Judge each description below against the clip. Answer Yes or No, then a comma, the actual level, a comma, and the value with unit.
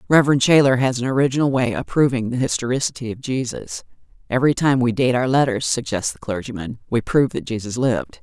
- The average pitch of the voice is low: Yes, low, 130 Hz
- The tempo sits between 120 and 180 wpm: No, average, 190 wpm